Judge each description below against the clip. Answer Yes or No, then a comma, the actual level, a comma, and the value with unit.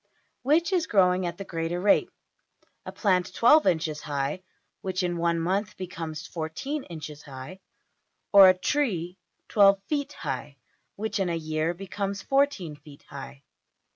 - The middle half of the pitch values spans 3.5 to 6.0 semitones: Yes, average, 3.9 semitones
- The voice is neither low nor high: Yes, medium, 180 Hz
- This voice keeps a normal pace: No, slow, 130 wpm